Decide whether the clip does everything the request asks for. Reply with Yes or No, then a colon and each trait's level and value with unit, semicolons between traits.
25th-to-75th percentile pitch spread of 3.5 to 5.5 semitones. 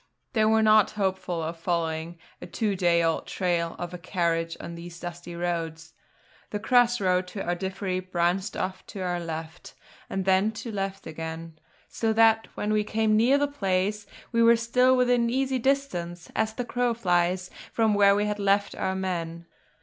Yes: average, 4.1 semitones